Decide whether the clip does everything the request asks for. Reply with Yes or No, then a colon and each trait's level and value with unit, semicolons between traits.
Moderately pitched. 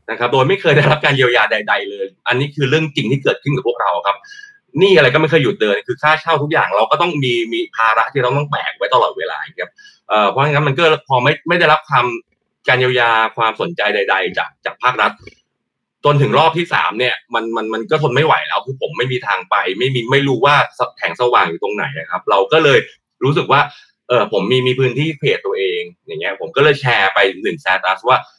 Yes: medium, 155 Hz